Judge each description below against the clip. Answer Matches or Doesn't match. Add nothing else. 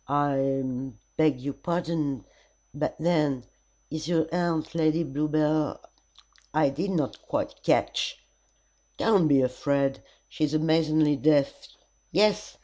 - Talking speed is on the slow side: Matches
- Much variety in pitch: Doesn't match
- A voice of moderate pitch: Matches